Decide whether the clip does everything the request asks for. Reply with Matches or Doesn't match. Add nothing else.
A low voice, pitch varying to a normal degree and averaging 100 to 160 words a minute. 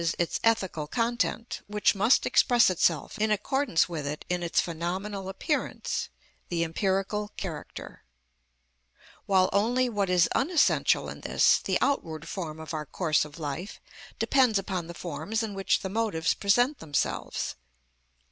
Doesn't match